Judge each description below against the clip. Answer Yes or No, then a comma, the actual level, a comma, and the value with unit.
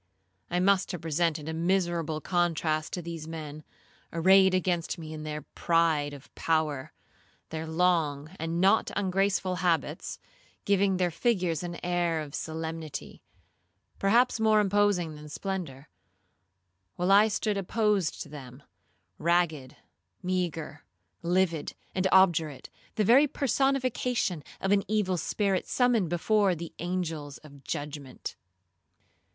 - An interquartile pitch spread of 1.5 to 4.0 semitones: Yes, average, 3.7 semitones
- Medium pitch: Yes, medium, 170 Hz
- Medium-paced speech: No, slow, 120 wpm